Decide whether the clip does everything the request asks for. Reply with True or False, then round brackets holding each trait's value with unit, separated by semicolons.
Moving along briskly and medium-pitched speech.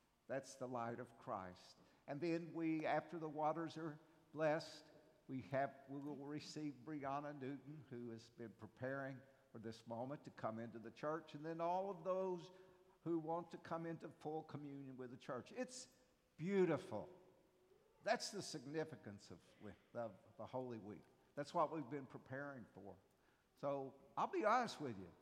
False (165 wpm; 145 Hz)